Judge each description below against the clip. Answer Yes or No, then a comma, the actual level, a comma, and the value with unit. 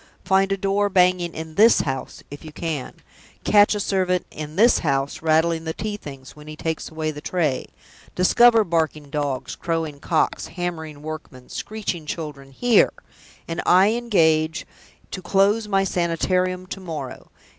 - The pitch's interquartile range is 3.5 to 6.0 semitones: Yes, average, 3.9 semitones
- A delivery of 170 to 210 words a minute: No, average, 155 wpm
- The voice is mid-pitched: Yes, medium, 165 Hz